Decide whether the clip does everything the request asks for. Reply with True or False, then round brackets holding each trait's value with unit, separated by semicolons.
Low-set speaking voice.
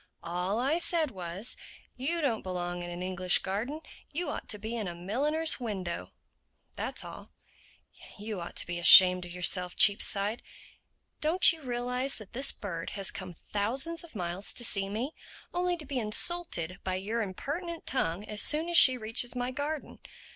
False (215 Hz)